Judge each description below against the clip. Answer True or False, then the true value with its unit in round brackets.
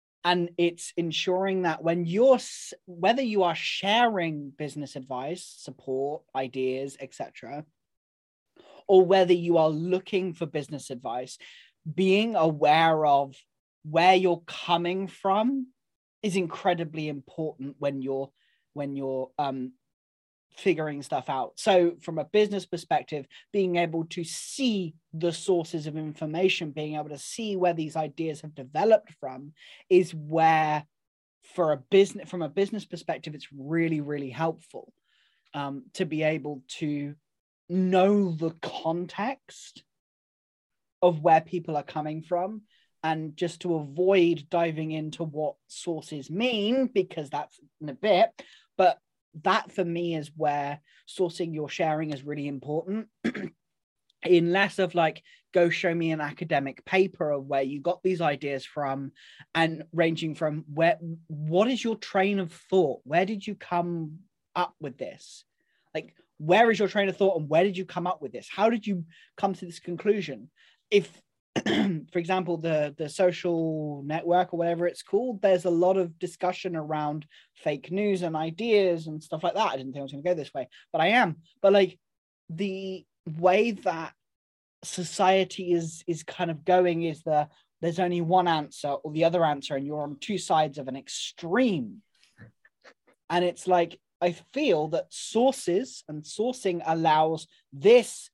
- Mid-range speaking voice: True (170 Hz)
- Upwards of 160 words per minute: False (155 wpm)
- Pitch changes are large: False (3.6 semitones)